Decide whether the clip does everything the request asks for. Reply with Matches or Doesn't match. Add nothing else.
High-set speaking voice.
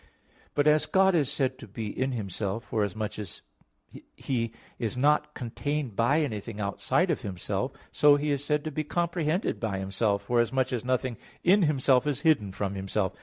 Doesn't match